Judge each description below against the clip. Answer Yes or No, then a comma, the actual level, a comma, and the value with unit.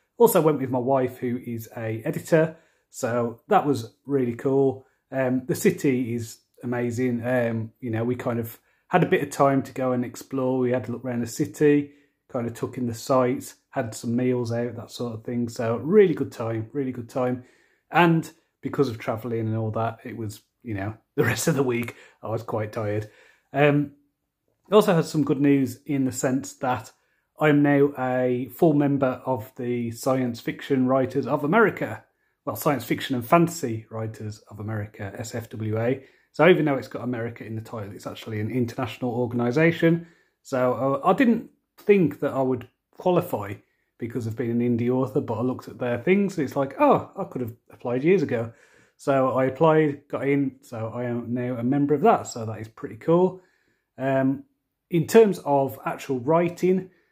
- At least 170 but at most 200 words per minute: Yes, average, 190 wpm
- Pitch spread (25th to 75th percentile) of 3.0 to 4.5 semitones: Yes, average, 3.4 semitones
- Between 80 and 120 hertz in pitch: No, low, 130 Hz